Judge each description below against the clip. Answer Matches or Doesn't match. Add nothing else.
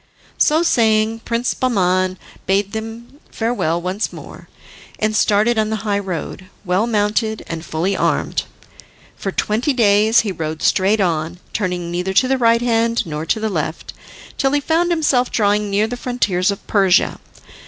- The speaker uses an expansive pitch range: Doesn't match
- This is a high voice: Matches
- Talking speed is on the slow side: Doesn't match